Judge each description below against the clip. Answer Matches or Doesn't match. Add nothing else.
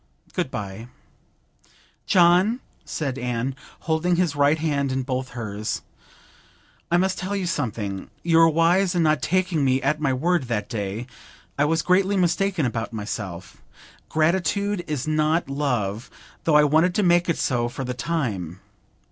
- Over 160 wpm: Doesn't match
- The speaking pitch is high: Doesn't match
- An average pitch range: Doesn't match